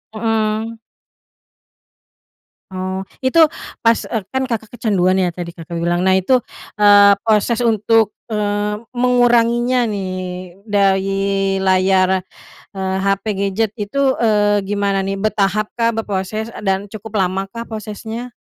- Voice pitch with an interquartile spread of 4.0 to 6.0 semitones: No, average, 2.7 semitones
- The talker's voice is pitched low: No, high, 210 Hz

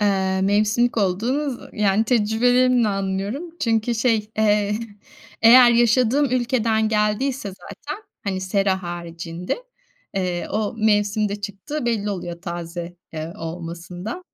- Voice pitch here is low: No, high, 210 Hz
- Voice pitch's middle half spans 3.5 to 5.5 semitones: Yes, average, 3.9 semitones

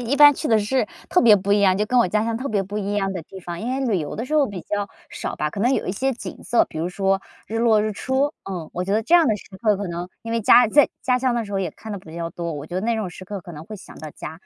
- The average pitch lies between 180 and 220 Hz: Yes, high, 205 Hz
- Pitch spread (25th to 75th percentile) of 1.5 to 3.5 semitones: No, average, 4.2 semitones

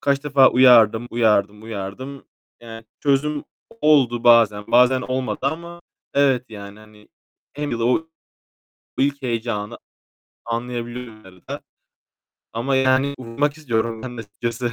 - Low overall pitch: Yes, low, 120 Hz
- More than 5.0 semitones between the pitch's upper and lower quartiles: No, average, 3.3 semitones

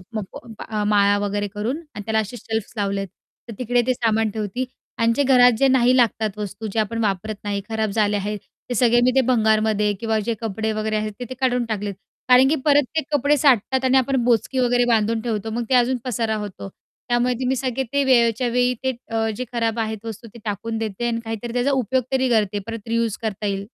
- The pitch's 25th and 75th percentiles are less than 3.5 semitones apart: Yes, average, 2.7 semitones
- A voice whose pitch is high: Yes, high, 230 Hz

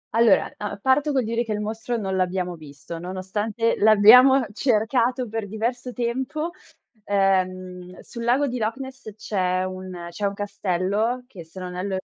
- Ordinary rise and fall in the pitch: Yes, average, 4.5 semitones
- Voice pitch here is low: No, high, 215 Hz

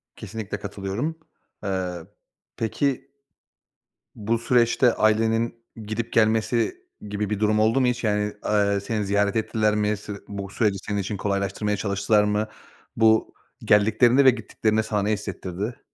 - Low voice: Yes, low, 105 Hz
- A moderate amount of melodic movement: No, narrow, 1.9 semitones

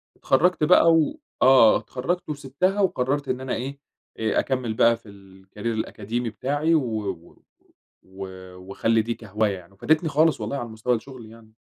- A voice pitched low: Yes, low, 125 Hz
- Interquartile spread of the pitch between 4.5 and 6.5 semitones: Yes, average, 4.8 semitones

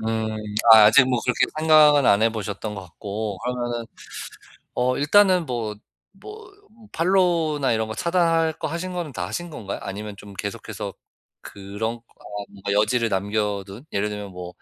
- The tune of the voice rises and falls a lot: Yes, wide, 7.3 semitones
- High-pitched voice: No, low, 115 Hz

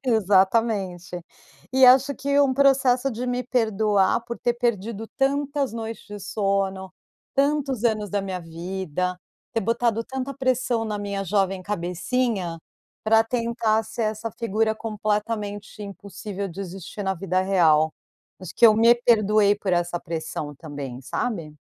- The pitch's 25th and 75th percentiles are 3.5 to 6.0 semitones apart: Yes, average, 3.9 semitones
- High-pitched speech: Yes, high, 210 Hz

